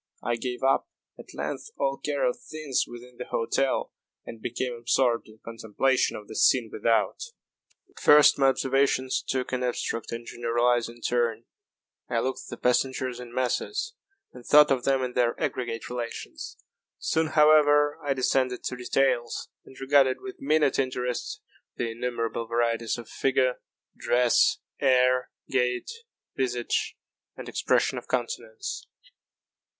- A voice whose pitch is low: Yes, low, 125 Hz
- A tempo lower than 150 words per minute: Yes, average, 140 wpm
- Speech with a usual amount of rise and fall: No, narrow, 2.3 semitones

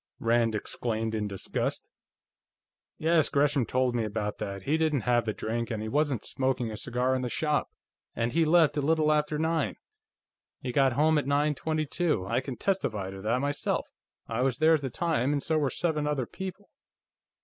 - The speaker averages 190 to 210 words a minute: Yes, average, 195 wpm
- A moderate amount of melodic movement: Yes, average, 4.9 semitones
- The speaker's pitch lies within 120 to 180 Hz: Yes, low, 135 Hz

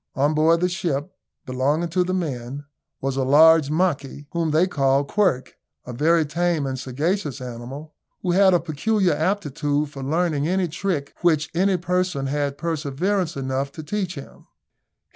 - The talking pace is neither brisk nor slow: Yes, average, 160 wpm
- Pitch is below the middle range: No, medium, 155 Hz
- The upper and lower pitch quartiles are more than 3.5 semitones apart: Yes, average, 4.2 semitones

